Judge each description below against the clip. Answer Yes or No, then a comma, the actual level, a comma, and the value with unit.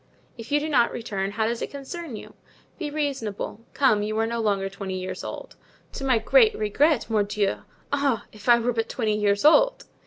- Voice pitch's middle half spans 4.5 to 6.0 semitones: Yes, average, 5.1 semitones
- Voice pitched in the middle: No, high, 230 Hz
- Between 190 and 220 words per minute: Yes, average, 195 wpm